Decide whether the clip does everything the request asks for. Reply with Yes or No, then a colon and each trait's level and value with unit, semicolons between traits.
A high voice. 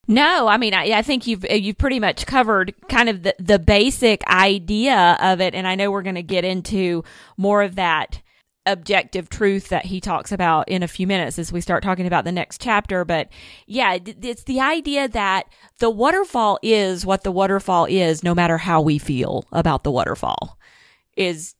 Yes: high, 195 Hz